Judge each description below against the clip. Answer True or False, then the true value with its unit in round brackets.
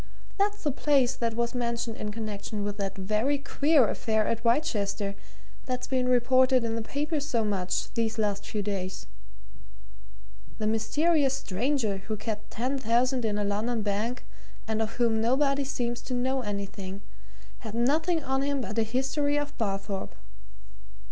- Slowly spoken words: False (155 wpm)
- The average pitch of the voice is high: True (235 Hz)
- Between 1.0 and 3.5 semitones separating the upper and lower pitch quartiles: False (4.0 semitones)